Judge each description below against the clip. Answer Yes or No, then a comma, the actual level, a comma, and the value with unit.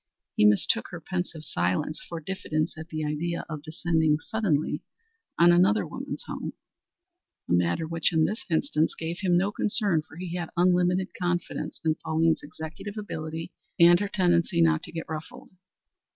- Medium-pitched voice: Yes, medium, 170 Hz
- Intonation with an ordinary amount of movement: No, narrow, 2.3 semitones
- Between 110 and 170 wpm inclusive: Yes, average, 160 wpm